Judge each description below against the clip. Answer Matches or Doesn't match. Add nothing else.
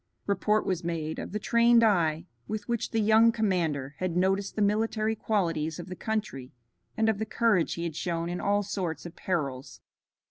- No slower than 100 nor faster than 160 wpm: Doesn't match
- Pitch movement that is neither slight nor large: Matches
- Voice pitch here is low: Doesn't match